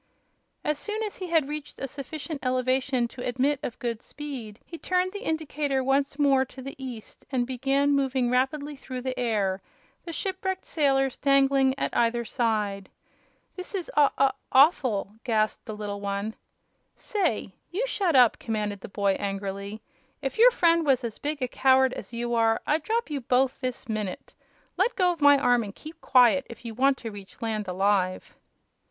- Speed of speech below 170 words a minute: No, average, 175 wpm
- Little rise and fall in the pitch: No, average, 4.6 semitones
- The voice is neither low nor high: No, very high, 260 Hz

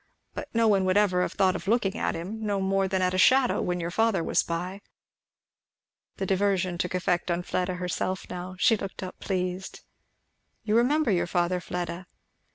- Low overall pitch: No, medium, 185 Hz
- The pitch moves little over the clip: Yes, narrow, 2.1 semitones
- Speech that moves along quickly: No, average, 185 wpm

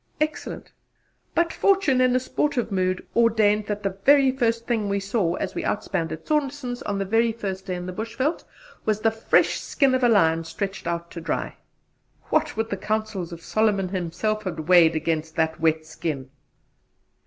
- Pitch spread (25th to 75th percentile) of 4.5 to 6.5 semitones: Yes, wide, 5.4 semitones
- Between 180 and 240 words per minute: Yes, average, 185 wpm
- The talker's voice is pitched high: Yes, high, 205 Hz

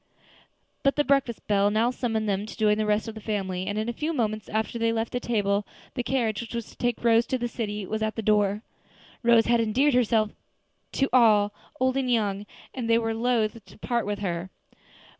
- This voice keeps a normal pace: No, fast, 215 wpm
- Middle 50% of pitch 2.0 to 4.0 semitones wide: Yes, narrow, 2.4 semitones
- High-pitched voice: Yes, high, 225 Hz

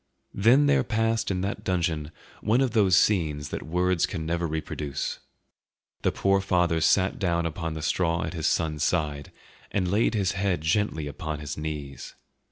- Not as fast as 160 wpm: No, average, 170 wpm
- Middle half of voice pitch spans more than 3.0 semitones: Yes, average, 4.0 semitones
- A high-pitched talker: No, very low, 85 Hz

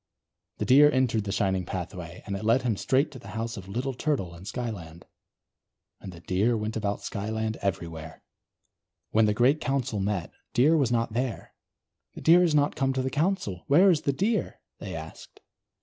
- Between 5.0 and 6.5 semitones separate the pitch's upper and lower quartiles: Yes, wide, 5.6 semitones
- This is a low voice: Yes, low, 115 Hz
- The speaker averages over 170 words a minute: Yes, average, 185 wpm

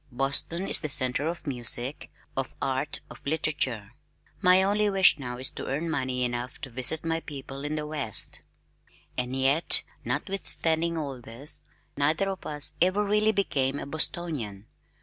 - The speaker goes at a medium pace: Yes, average, 155 wpm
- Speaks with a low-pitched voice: No, medium, 145 Hz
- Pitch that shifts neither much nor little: Yes, average, 4.4 semitones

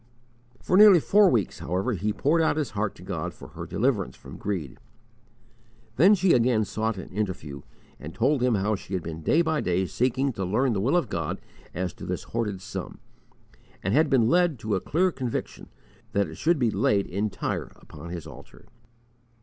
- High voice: No, low, 110 Hz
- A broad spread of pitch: Yes, wide, 7.2 semitones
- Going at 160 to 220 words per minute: Yes, average, 190 wpm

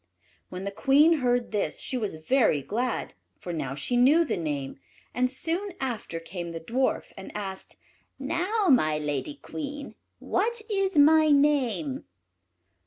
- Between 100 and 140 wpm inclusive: No, average, 150 wpm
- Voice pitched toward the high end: Yes, very high, 255 Hz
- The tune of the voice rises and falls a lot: Yes, wide, 8.6 semitones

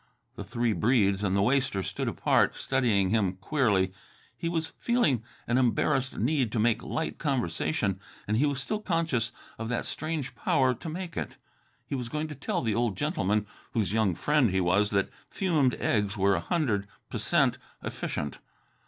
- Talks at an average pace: Yes, average, 170 wpm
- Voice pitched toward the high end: No, low, 120 Hz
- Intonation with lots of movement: Yes, wide, 6.6 semitones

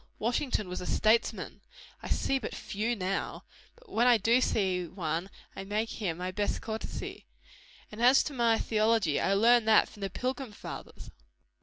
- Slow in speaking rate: No, average, 170 wpm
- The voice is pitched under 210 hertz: No, high, 215 Hz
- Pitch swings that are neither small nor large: Yes, average, 3.6 semitones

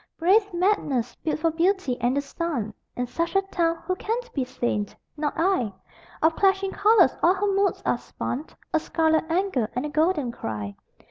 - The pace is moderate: Yes, average, 180 wpm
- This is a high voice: Yes, very high, 325 Hz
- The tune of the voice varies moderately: No, wide, 7.0 semitones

